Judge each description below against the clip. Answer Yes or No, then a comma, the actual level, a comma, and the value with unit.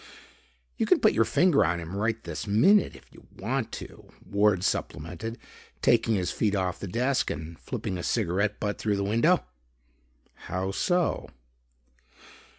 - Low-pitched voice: Yes, low, 100 Hz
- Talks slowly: No, average, 155 wpm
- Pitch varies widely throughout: No, average, 4.0 semitones